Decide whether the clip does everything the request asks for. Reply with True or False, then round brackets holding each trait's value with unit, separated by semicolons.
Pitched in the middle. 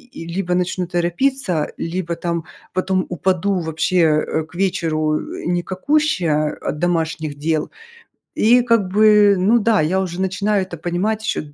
True (180 Hz)